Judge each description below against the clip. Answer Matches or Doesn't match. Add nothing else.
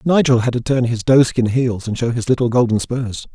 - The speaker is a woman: Doesn't match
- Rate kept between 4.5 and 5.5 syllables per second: Matches